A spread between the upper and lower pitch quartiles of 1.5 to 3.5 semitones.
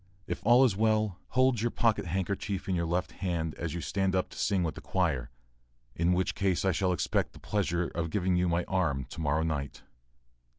Yes: average, 3.0 semitones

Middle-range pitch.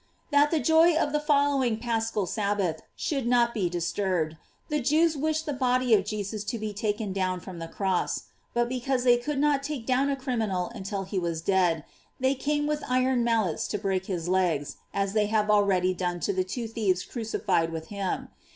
No: high, 215 Hz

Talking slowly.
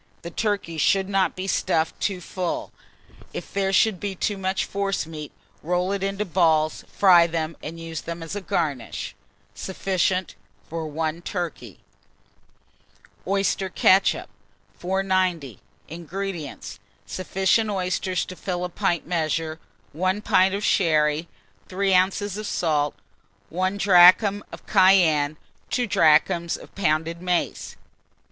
Yes: slow, 125 wpm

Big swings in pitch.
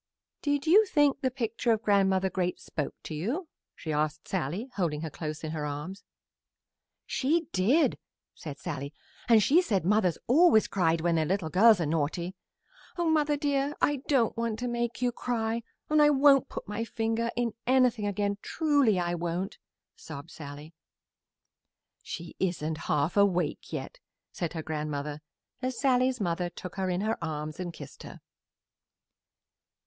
Yes: wide, 7.4 semitones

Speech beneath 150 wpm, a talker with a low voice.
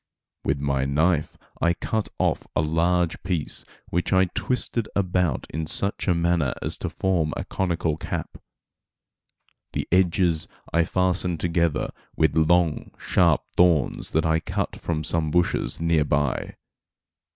Yes: average, 140 wpm; very low, 85 Hz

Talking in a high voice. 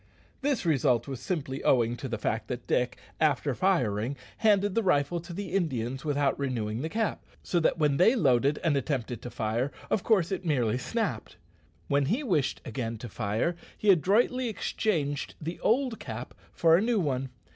No: medium, 145 Hz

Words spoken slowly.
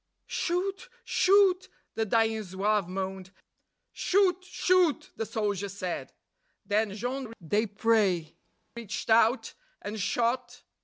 Yes: slow, 100 wpm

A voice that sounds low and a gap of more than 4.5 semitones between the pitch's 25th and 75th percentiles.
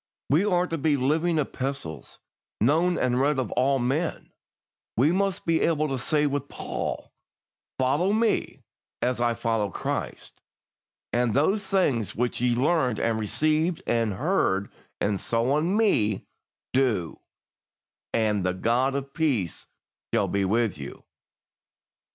Yes: low, 130 Hz; wide, 5.6 semitones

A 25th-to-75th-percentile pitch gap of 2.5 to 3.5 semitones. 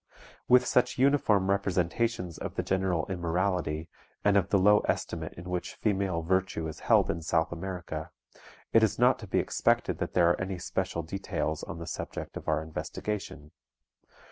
Yes: average, 3.2 semitones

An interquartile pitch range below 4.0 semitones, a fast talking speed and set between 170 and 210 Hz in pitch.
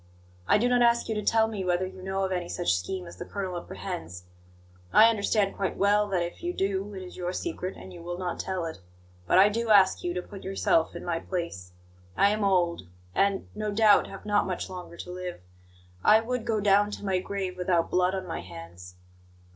Yes: average, 2.8 semitones; fast, 220 wpm; high, 190 Hz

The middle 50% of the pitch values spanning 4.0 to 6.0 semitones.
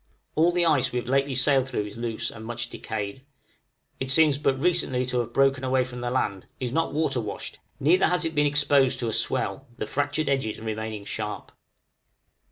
No: average, 3.6 semitones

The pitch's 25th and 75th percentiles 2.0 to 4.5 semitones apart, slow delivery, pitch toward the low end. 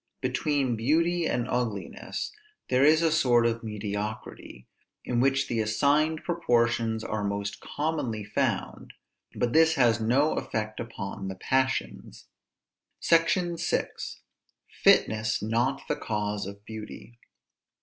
No: average, 5.0 semitones; slow, 120 wpm; low, 120 Hz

